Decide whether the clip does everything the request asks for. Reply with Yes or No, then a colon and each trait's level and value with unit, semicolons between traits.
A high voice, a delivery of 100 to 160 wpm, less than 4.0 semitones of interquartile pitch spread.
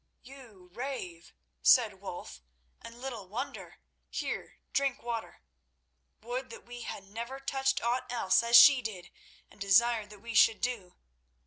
Yes: high, 235 Hz; average, 140 wpm; average, 3.6 semitones